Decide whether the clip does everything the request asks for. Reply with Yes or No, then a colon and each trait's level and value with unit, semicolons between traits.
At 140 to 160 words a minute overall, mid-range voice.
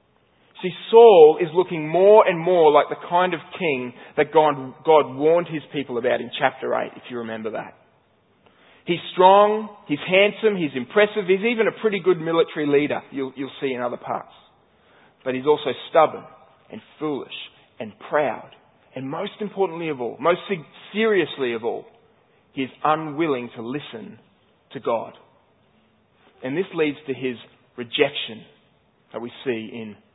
Yes: average, 155 wpm; medium, 160 Hz